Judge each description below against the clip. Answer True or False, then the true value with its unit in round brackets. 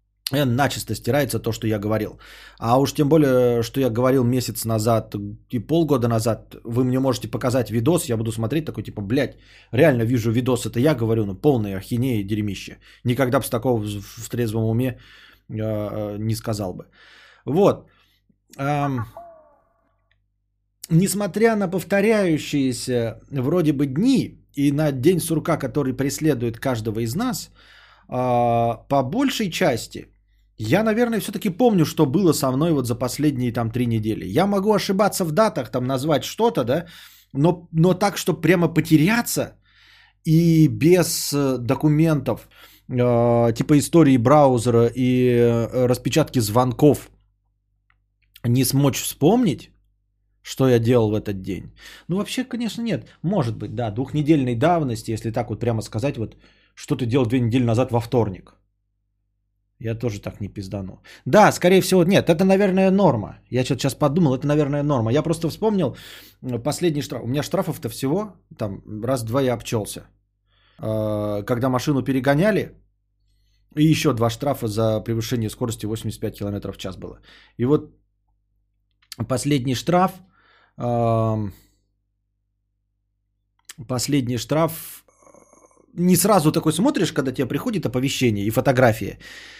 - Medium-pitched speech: False (125 Hz)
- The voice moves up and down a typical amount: False (5.8 semitones)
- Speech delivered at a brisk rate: False (140 wpm)